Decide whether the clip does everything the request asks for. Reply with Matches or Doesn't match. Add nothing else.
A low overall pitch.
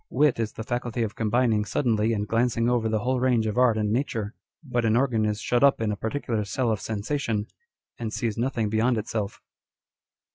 Matches